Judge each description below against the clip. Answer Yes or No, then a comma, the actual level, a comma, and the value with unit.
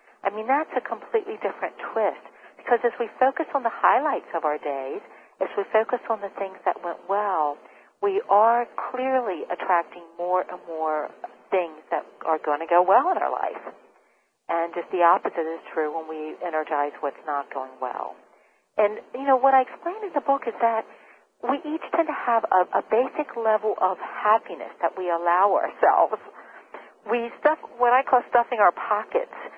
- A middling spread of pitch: No, wide, 7.2 semitones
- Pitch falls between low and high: No, high, 210 Hz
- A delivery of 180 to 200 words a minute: Yes, average, 185 wpm